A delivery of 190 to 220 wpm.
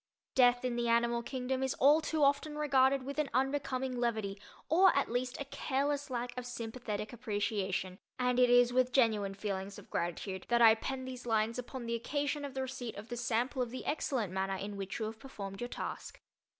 Yes: average, 200 wpm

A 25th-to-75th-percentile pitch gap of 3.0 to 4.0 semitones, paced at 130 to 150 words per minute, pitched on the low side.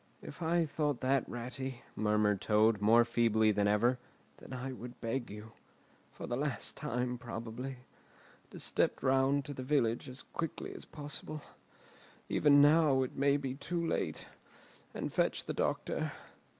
Yes: average, 3.6 semitones; slow, 135 wpm; low, 130 Hz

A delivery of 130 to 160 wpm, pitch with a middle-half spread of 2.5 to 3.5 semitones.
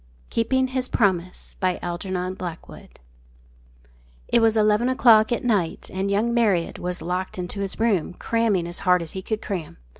No: average, 145 wpm; average, 4.0 semitones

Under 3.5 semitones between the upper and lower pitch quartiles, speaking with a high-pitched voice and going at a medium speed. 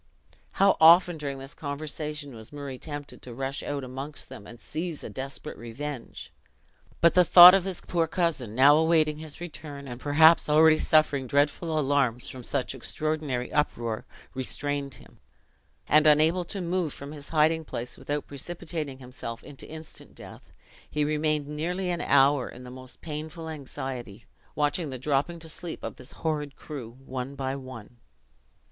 No: average, 3.1 semitones; medium, 145 Hz; average, 160 wpm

